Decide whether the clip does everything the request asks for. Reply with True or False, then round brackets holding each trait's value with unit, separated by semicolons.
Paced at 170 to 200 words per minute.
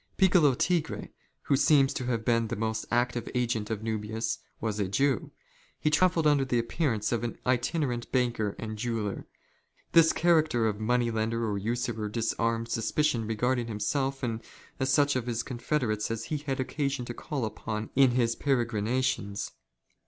False (160 wpm)